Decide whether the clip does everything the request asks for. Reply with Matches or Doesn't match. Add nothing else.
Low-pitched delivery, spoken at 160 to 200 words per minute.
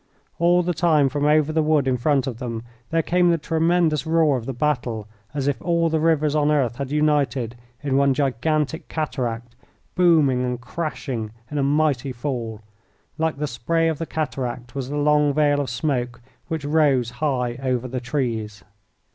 Doesn't match